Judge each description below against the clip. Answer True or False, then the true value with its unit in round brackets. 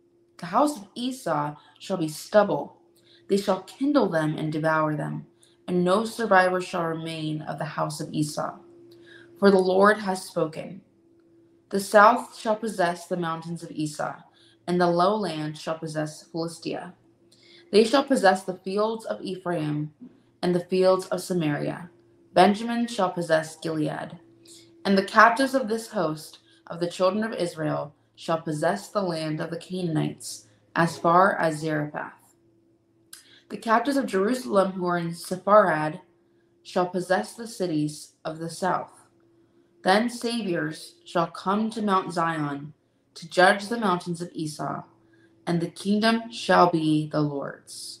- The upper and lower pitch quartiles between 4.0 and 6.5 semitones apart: True (4.6 semitones)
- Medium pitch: True (180 Hz)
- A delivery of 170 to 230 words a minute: False (145 wpm)